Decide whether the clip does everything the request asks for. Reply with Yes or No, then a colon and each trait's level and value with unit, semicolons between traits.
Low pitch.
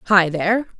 No: high, 195 Hz